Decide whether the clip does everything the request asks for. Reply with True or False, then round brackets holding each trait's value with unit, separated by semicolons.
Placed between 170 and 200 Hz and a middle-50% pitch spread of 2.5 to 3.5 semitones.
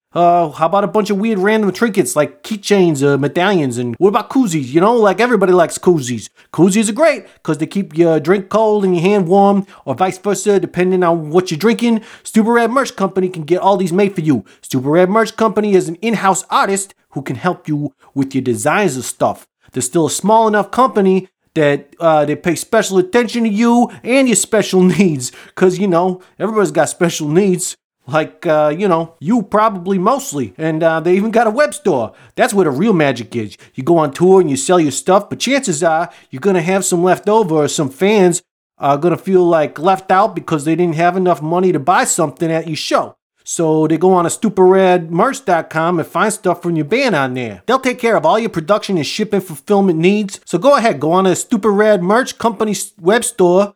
False (185 Hz; 4.5 semitones)